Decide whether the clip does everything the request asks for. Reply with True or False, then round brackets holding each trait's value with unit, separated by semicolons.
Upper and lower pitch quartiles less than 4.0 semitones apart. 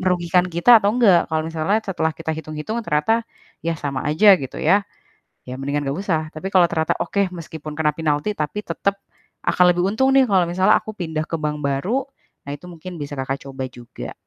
False (4.3 semitones)